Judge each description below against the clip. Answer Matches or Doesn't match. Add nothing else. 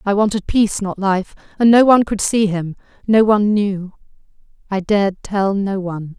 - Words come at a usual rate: Matches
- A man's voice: Doesn't match